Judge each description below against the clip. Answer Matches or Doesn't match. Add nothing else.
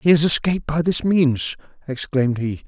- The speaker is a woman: Doesn't match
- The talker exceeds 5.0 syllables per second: Matches